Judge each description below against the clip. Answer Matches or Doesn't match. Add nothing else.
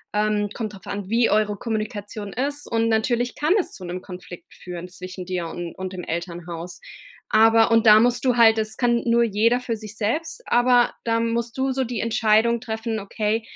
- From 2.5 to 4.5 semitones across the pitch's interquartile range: Matches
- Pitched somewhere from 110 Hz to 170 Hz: Doesn't match